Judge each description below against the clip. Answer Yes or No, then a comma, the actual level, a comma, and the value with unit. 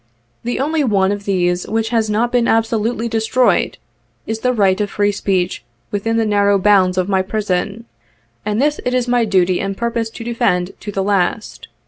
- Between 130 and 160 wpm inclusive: No, average, 185 wpm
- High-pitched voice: Yes, high, 210 Hz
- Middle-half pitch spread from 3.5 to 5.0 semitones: No, average, 2.9 semitones